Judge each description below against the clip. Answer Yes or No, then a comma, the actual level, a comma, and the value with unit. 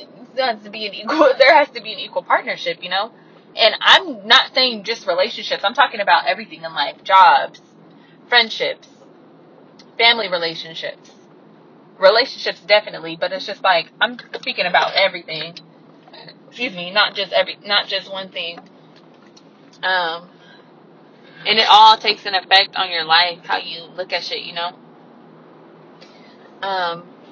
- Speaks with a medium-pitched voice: No, high, 195 Hz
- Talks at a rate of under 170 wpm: Yes, average, 150 wpm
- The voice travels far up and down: No, average, 4.7 semitones